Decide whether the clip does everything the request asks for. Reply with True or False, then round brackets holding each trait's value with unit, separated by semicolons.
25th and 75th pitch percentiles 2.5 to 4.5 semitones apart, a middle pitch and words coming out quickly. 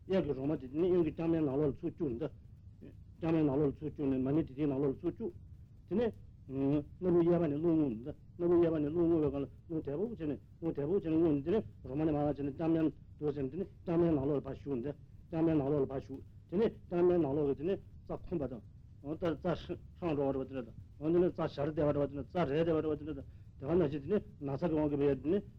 True (3.4 semitones; 150 Hz; 190 wpm)